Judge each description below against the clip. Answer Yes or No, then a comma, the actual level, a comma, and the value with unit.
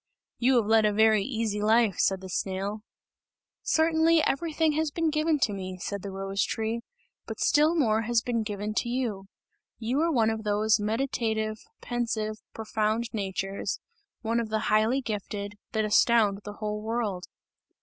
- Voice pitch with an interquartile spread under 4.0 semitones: Yes, average, 2.7 semitones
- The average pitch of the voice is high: Yes, high, 220 Hz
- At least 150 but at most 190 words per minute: Yes, average, 160 wpm